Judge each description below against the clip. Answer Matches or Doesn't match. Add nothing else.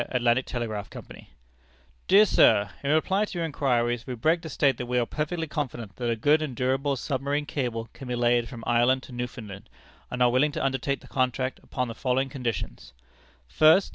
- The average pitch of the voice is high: Doesn't match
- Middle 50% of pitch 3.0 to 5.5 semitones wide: Matches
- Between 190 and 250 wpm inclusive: Matches